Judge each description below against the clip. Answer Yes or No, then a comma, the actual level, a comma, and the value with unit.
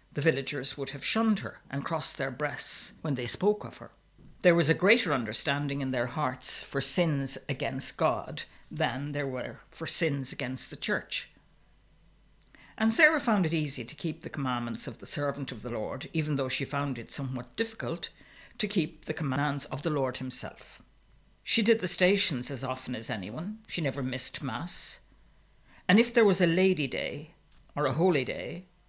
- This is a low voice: No, medium, 145 Hz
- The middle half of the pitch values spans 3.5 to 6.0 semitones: Yes, average, 4.4 semitones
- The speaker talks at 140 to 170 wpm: No, average, 185 wpm